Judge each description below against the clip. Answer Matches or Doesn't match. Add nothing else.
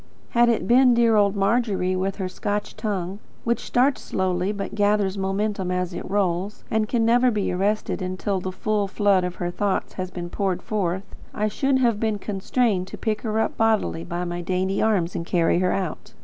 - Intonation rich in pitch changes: Doesn't match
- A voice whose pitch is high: Matches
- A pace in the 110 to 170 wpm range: Doesn't match